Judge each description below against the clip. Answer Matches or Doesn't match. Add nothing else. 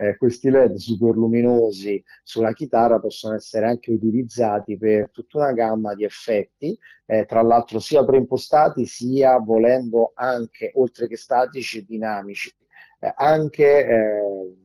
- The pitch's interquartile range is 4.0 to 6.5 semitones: Doesn't match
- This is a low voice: Matches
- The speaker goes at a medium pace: Matches